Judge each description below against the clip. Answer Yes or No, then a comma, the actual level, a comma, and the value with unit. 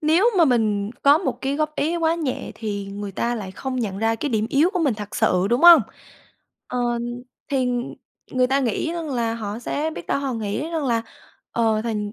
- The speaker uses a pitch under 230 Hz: No, high, 245 Hz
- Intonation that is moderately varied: No, wide, 5.8 semitones